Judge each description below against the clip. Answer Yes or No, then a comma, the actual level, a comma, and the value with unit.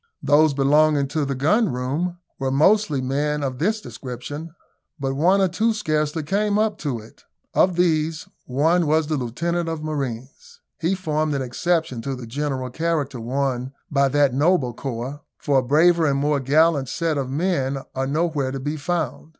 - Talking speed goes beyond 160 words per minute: Yes, average, 175 wpm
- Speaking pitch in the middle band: Yes, medium, 150 Hz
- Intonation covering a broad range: No, average, 3.7 semitones